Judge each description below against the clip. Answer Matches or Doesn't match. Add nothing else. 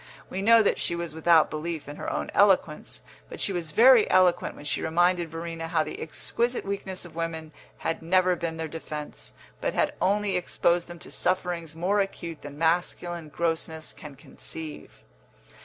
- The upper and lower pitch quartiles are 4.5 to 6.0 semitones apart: Doesn't match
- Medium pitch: Matches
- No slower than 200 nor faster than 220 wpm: Doesn't match